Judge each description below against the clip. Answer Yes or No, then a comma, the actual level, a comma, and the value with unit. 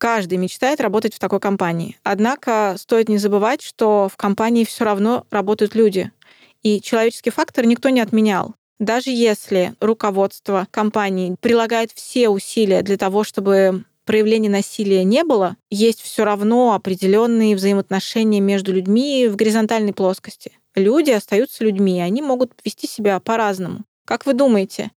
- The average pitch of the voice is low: No, high, 215 Hz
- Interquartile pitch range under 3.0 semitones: Yes, narrow, 2.4 semitones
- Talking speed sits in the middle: Yes, average, 140 wpm